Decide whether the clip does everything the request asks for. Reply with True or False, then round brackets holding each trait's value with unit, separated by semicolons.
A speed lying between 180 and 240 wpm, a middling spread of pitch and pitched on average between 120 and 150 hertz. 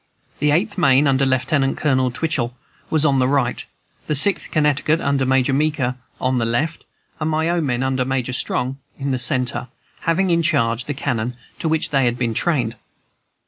True (185 wpm; 3.5 semitones; 135 Hz)